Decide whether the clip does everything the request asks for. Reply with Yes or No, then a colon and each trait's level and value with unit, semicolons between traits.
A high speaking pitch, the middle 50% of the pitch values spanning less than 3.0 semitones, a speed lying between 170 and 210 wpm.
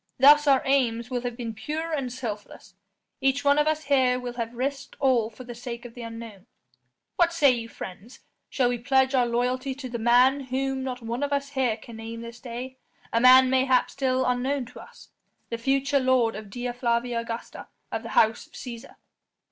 Yes: very high, 250 Hz; narrow, 2.4 semitones; average, 200 wpm